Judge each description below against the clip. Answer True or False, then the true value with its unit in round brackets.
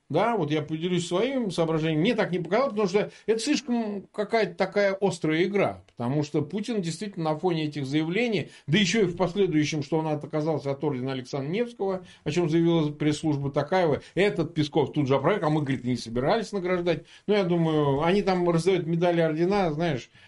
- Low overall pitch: False (170 Hz)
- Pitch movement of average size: True (4.6 semitones)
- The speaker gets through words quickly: True (185 wpm)